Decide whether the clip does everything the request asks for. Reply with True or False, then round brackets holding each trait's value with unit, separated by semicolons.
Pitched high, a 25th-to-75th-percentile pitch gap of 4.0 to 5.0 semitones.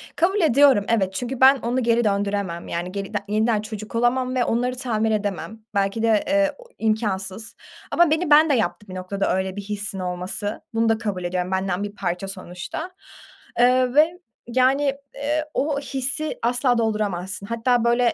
True (225 Hz; 4.5 semitones)